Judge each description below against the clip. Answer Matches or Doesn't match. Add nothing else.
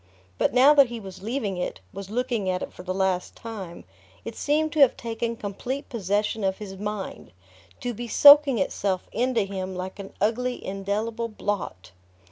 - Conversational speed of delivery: Matches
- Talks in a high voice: Matches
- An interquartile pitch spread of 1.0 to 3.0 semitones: Doesn't match